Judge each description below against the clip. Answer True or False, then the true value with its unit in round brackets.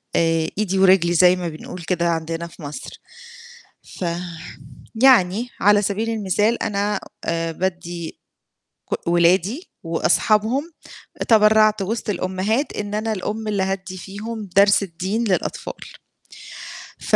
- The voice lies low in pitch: False (195 Hz)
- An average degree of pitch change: True (3.5 semitones)